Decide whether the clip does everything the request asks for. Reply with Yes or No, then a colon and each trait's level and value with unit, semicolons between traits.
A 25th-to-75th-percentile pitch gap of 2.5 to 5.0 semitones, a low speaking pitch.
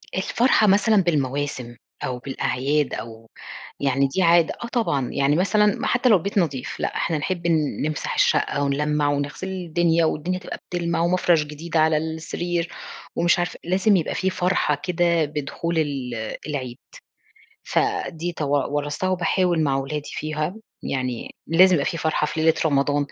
No: average, 3.6 semitones; medium, 160 Hz